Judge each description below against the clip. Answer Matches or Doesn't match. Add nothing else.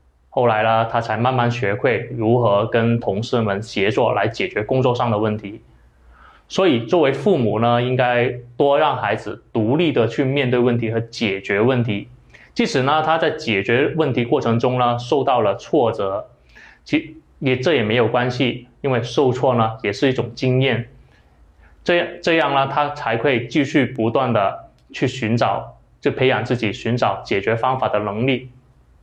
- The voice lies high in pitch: Doesn't match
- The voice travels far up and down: Doesn't match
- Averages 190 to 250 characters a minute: Matches